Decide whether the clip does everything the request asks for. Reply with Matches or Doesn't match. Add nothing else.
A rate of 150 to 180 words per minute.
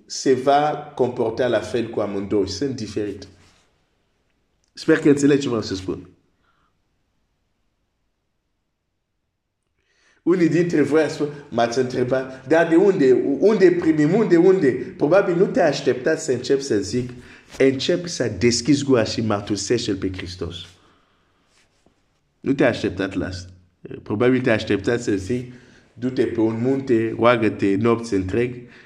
Doesn't match